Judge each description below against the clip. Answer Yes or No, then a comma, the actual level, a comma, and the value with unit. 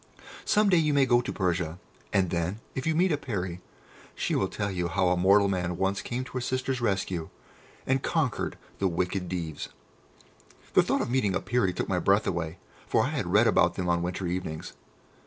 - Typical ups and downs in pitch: No, wide, 5.9 semitones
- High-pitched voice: No, very low, 95 Hz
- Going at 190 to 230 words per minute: Yes, fast, 205 wpm